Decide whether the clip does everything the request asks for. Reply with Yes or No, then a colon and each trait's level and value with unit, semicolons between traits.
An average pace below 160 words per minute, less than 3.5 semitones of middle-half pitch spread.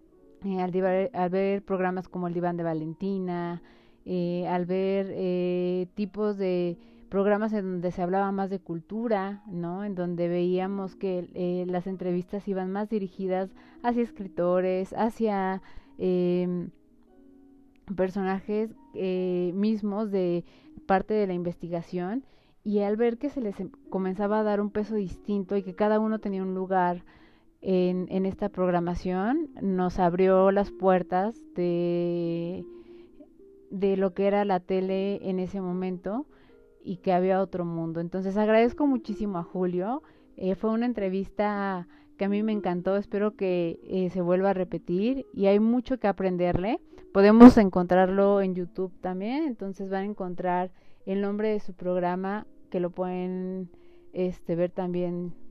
Yes: average, 150 wpm; narrow, 2.5 semitones